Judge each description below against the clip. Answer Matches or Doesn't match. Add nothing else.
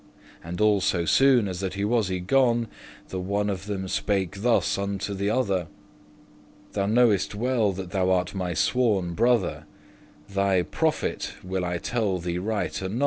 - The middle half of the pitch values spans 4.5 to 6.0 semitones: Doesn't match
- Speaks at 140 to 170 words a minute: Matches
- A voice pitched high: Doesn't match